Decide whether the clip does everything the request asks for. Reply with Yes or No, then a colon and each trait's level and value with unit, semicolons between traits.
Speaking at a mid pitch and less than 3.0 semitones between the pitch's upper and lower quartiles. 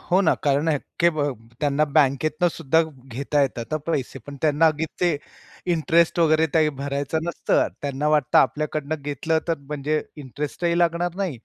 Yes: medium, 155 Hz; narrow, 2.5 semitones